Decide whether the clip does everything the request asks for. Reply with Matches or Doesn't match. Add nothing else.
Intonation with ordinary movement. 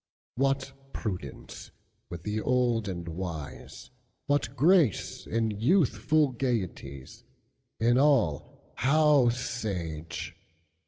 Doesn't match